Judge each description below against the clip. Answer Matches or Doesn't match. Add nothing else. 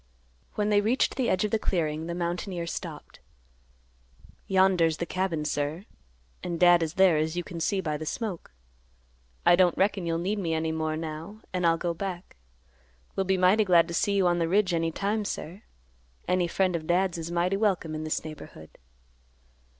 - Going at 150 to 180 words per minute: Doesn't match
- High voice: Doesn't match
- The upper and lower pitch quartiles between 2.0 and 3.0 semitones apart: Matches